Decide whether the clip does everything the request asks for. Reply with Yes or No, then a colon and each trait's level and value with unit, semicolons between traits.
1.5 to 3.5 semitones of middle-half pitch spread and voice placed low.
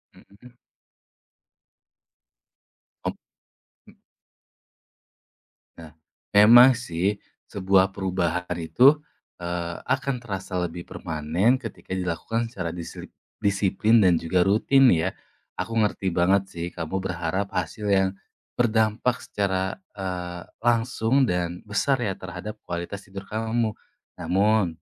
No: average, 4.1 semitones; very low, 95 Hz